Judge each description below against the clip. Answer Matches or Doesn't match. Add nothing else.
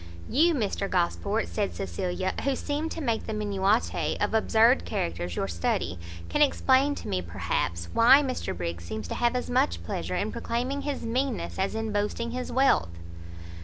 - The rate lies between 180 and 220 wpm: Doesn't match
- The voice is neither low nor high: Doesn't match